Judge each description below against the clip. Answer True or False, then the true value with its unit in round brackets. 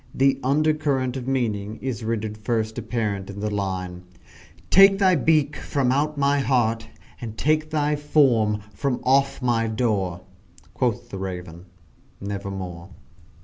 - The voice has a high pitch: False (120 Hz)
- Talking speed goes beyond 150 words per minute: False (140 wpm)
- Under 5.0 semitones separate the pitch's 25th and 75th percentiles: False (5.3 semitones)